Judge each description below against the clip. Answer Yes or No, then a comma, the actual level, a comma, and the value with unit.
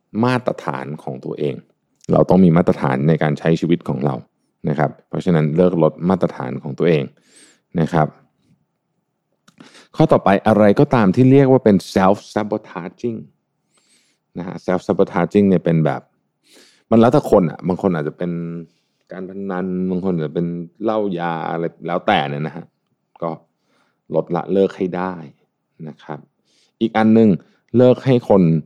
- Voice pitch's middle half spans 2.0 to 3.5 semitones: No, average, 4.7 semitones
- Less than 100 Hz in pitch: Yes, very low, 90 Hz